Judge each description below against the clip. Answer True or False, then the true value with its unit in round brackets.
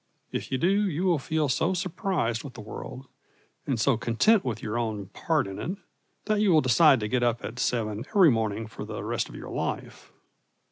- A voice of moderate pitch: False (130 Hz)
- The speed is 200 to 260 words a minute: True (205 wpm)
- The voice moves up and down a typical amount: False (7.3 semitones)